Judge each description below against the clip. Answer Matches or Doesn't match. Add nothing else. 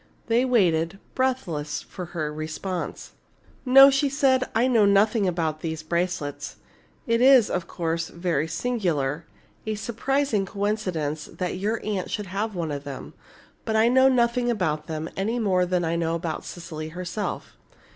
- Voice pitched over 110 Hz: Matches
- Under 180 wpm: Matches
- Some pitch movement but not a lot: Doesn't match